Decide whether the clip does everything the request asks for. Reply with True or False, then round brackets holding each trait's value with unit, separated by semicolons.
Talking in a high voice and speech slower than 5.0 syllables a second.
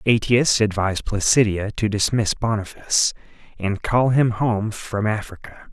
False (110 Hz; 4.5 syllables/s)